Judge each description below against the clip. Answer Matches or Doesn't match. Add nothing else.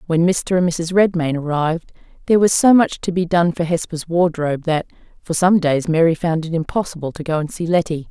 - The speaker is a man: Doesn't match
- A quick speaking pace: Matches